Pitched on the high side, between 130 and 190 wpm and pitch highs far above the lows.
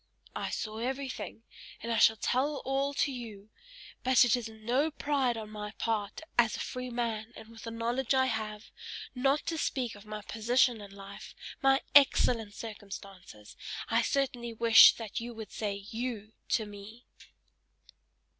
No: high, 230 Hz; average, 160 wpm; average, 3.0 semitones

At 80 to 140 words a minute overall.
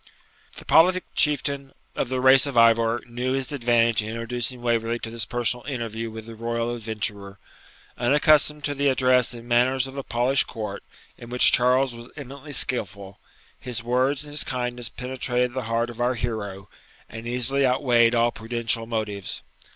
No: average, 165 wpm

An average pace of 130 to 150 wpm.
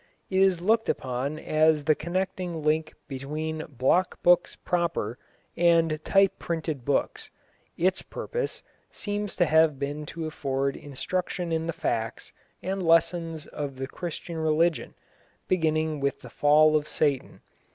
Yes: slow, 135 wpm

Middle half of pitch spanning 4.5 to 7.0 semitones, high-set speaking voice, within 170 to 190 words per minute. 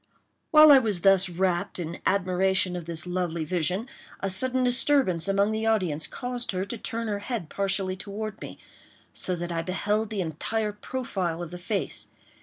No: average, 3.7 semitones; high, 195 Hz; average, 175 wpm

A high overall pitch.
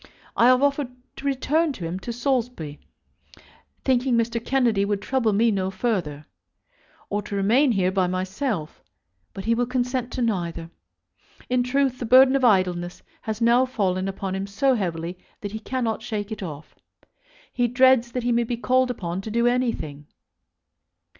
Yes: high, 230 Hz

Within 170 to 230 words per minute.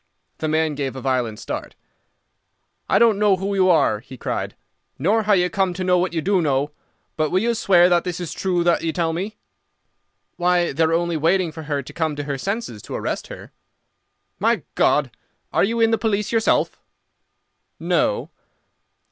Yes: average, 190 wpm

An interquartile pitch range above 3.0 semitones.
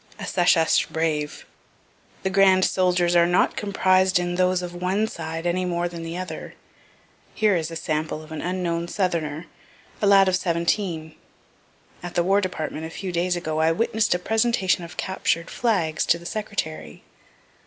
No: narrow, 2.4 semitones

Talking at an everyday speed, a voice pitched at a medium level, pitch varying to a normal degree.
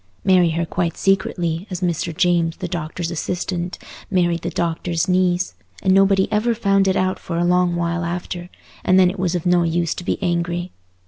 No: average, 190 wpm; medium, 175 Hz; narrow, 1.5 semitones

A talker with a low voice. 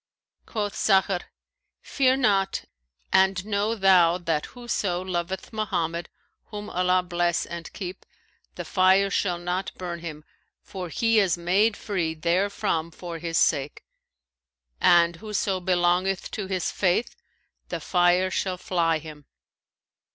No: medium, 185 Hz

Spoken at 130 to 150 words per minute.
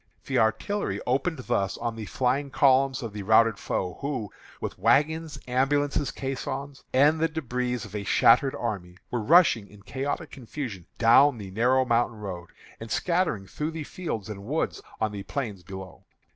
No: average, 165 wpm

